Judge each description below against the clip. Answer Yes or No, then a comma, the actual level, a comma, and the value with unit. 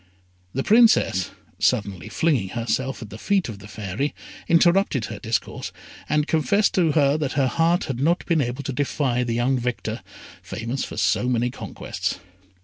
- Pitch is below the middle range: Yes, low, 130 Hz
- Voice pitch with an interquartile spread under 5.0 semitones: No, wide, 5.4 semitones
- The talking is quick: No, average, 165 wpm